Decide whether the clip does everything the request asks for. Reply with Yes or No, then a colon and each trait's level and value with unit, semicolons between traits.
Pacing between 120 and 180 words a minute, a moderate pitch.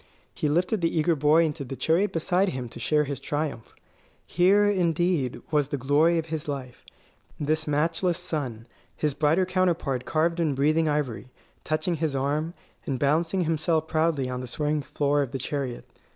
Yes: average, 170 wpm; medium, 155 Hz